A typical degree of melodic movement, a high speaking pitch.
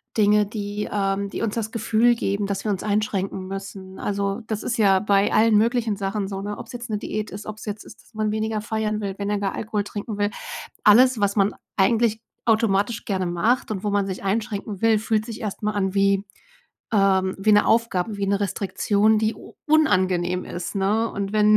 No: narrow, 1.7 semitones; high, 205 Hz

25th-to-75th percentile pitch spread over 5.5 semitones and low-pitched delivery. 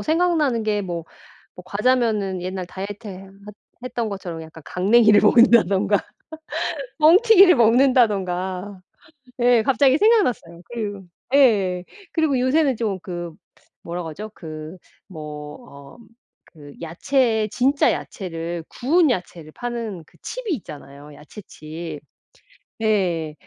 No: wide, 6.1 semitones; high, 205 Hz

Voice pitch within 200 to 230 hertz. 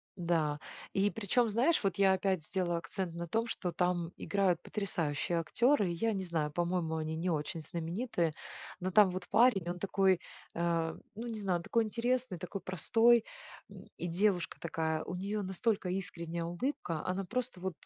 No: medium, 185 Hz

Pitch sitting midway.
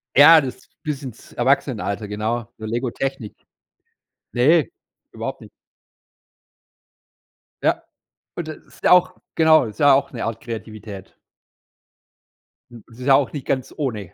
No: low, 125 Hz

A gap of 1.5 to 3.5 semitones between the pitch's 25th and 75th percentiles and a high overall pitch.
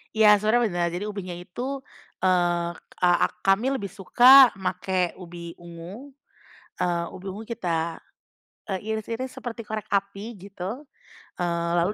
No: average, 4.1 semitones; high, 195 Hz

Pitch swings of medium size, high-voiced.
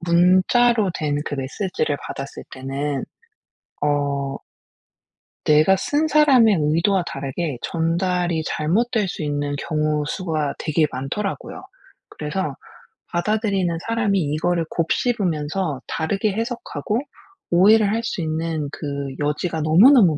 No: average, 5.0 semitones; medium, 165 Hz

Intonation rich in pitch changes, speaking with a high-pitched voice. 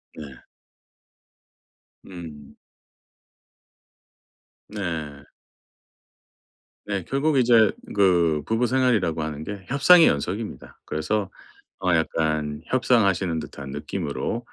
No: wide, 6.5 semitones; very low, 95 Hz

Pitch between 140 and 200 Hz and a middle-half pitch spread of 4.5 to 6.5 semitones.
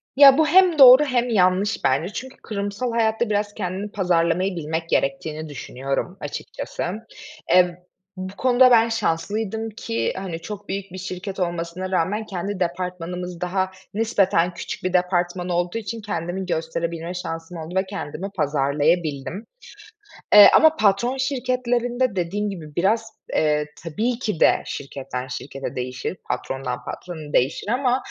Yes: medium, 185 Hz; average, 4.8 semitones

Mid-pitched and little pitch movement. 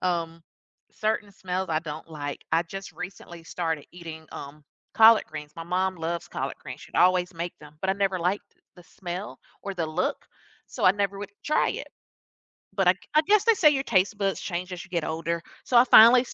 No: medium, 180 Hz; average, 3.2 semitones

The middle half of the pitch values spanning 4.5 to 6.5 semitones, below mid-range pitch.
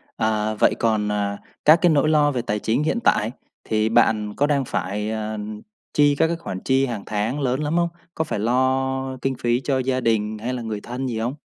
No: average, 3.9 semitones; low, 120 Hz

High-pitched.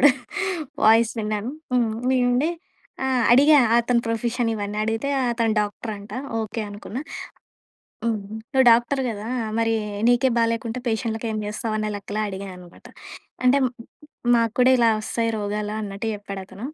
Yes: high, 225 Hz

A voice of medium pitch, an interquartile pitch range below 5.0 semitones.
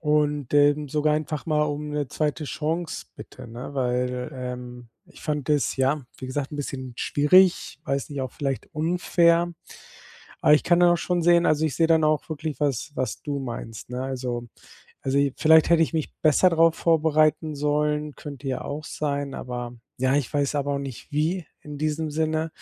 Yes: medium, 150 Hz; average, 2.7 semitones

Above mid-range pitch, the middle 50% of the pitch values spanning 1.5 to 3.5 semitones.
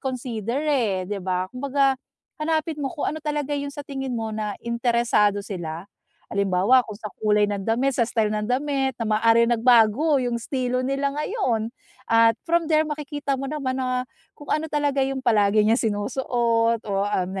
No: high, 245 Hz; average, 4.3 semitones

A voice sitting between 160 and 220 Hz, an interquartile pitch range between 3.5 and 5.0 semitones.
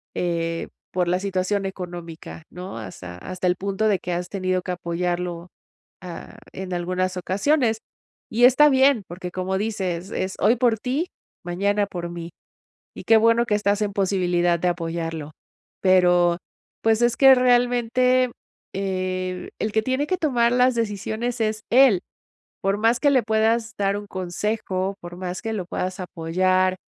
Yes: high, 190 Hz; average, 4.1 semitones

